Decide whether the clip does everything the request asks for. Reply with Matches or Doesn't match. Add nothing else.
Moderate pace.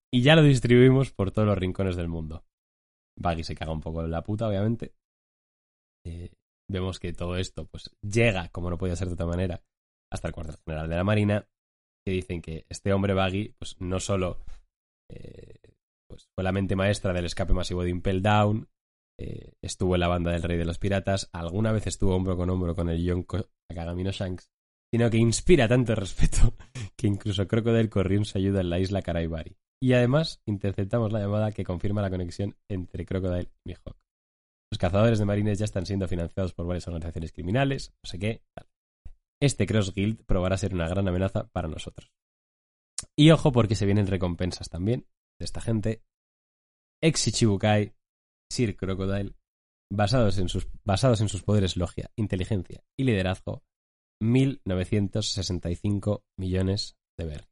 Matches